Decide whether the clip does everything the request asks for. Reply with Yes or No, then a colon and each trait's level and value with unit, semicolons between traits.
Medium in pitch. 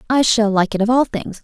No: high, 220 Hz